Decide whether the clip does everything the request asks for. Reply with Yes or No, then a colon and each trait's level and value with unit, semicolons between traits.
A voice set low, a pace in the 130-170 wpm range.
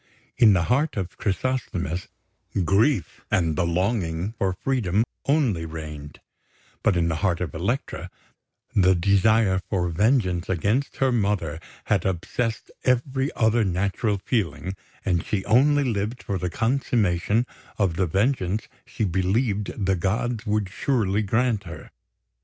Yes: low, 100 Hz; slow, 135 wpm